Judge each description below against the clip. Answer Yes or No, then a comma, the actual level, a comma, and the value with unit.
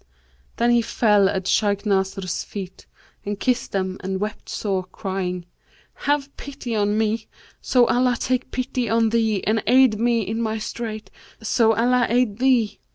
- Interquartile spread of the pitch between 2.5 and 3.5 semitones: Yes, average, 3.1 semitones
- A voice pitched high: Yes, high, 220 Hz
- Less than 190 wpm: Yes, average, 160 wpm